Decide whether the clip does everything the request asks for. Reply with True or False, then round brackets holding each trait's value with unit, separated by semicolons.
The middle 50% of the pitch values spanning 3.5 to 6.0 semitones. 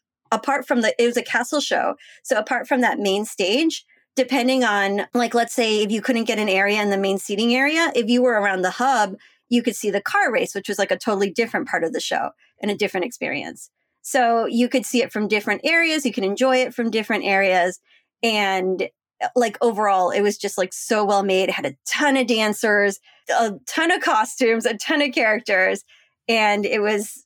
True (3.8 semitones)